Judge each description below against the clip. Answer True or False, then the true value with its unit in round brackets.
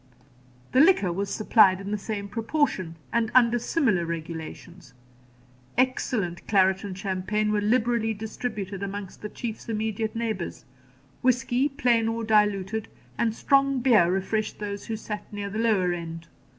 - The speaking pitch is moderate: False (210 Hz)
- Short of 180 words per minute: True (140 wpm)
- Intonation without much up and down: False (3.2 semitones)